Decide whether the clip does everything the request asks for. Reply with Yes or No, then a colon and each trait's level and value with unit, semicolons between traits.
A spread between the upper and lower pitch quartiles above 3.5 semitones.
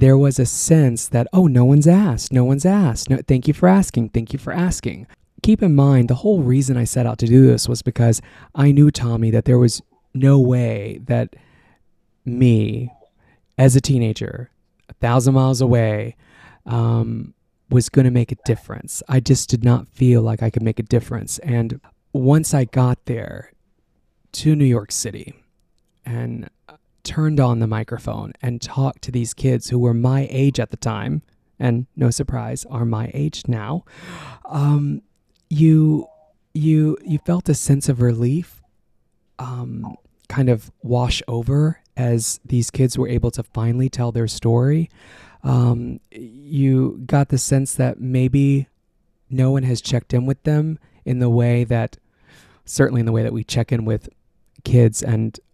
No: average, 2.8 semitones